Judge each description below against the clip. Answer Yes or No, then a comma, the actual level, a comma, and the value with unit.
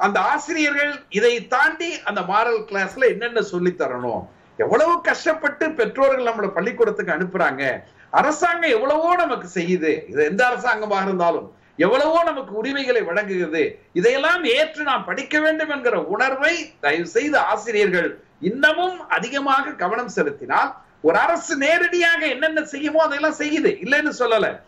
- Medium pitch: No, very high, 285 Hz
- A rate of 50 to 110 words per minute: No, average, 125 wpm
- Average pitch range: No, wide, 6.7 semitones